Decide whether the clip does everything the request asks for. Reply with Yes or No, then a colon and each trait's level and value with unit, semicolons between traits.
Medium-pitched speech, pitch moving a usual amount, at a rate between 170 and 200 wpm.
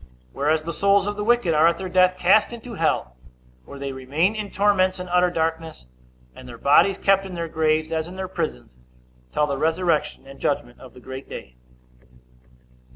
Yes: medium, 165 Hz; average, 4.6 semitones; average, 190 wpm